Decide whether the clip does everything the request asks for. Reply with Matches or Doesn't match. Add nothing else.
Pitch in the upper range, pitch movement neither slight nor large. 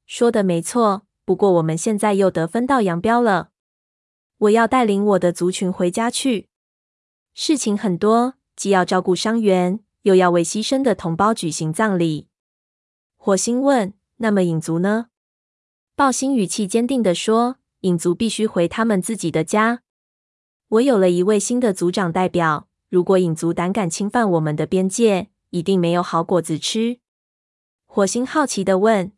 Matches